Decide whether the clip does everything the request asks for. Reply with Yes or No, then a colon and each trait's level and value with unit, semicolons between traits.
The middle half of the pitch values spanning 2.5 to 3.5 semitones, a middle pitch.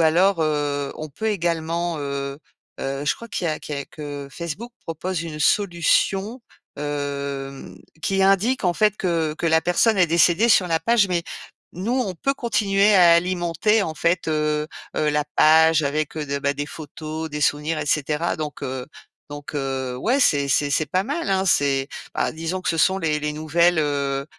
No: average, 3.9 semitones; medium, 160 Hz